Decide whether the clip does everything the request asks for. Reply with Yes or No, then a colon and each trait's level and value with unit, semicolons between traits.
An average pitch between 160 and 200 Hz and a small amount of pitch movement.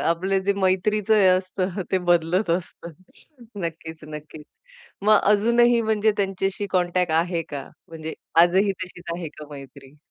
No: medium, 185 Hz; average, 3.2 semitones